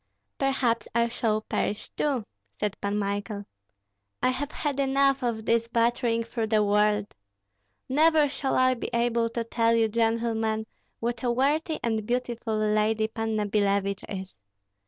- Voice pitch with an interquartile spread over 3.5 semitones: No, narrow, 2.6 semitones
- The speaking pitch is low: No, high, 230 Hz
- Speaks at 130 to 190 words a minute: Yes, average, 145 wpm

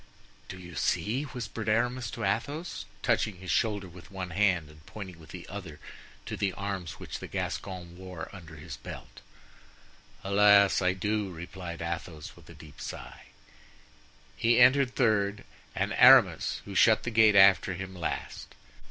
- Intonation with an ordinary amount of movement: Yes, average, 3.3 semitones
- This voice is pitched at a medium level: No, very low, 95 Hz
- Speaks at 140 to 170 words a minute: Yes, average, 155 wpm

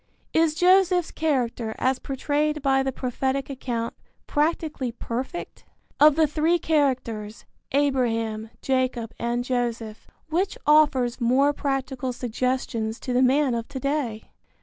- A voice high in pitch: Yes, very high, 265 Hz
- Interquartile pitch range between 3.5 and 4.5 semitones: Yes, average, 3.8 semitones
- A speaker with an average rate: No, slow, 125 wpm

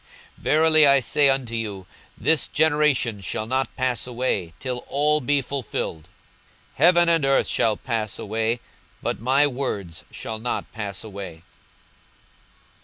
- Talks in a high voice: No, low, 125 Hz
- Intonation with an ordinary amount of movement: Yes, average, 4.6 semitones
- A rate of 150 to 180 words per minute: No, average, 140 wpm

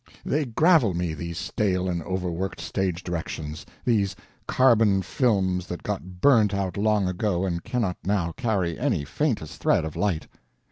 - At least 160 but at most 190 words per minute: No, average, 150 wpm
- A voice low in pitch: Yes, very low, 95 Hz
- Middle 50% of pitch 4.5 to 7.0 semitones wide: No, average, 3.7 semitones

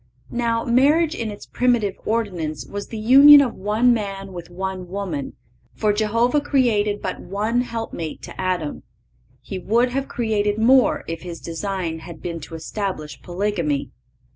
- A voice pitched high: Yes, high, 205 Hz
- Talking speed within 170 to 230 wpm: No, average, 150 wpm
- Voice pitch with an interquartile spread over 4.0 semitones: Yes, average, 4.8 semitones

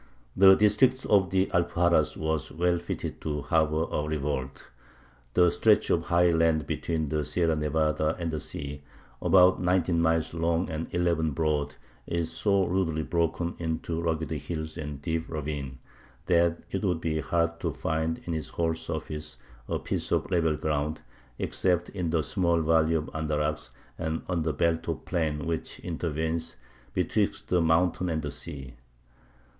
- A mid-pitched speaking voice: No, very low, 80 Hz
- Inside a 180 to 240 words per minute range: No, average, 160 wpm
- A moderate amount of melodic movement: No, narrow, 1.9 semitones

